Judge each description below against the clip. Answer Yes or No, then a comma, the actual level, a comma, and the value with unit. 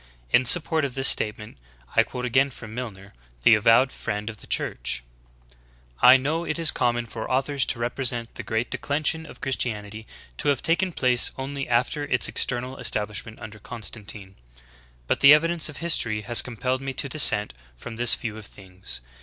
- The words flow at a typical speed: Yes, average, 180 wpm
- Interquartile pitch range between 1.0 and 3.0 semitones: No, average, 4.0 semitones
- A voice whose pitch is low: Yes, low, 125 Hz